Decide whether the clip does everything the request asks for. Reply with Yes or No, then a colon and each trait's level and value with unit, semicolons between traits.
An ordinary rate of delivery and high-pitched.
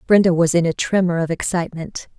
No: average, 190 wpm; medium, 170 Hz